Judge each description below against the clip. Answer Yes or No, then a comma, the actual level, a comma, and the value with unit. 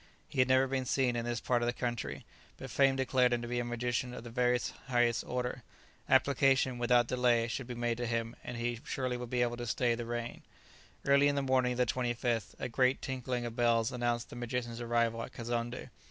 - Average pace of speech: No, fast, 220 wpm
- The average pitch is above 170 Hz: No, low, 120 Hz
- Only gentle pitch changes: Yes, narrow, 1.1 semitones